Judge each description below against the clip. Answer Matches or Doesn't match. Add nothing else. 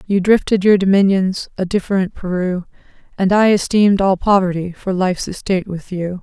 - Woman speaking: Matches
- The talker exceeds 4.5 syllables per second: Matches